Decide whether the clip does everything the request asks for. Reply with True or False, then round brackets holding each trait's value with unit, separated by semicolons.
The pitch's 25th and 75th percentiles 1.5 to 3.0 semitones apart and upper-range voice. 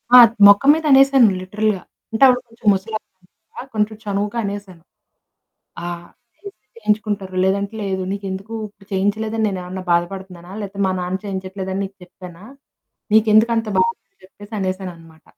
True (2.5 semitones; 200 Hz)